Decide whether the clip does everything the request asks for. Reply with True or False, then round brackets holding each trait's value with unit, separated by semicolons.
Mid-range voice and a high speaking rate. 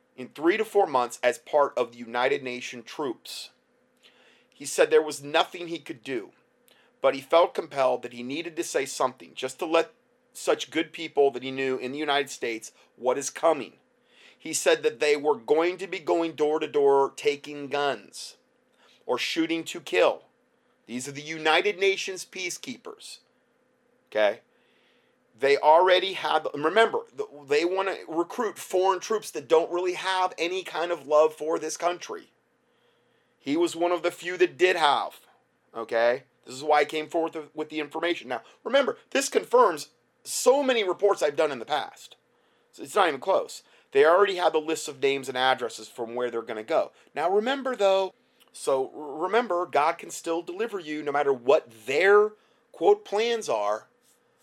False (170 Hz; 175 wpm)